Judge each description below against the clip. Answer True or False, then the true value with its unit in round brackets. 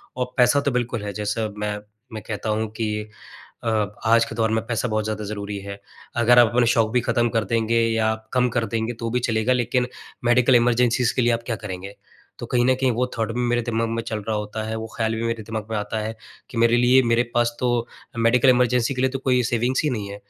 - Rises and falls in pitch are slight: True (1.8 semitones)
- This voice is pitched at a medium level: False (115 Hz)